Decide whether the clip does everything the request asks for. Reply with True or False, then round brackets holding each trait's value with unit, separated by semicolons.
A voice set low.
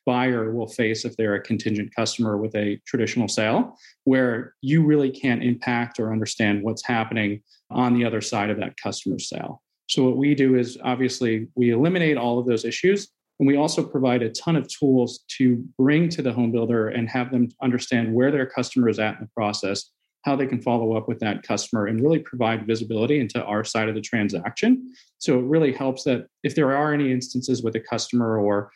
True (120 Hz)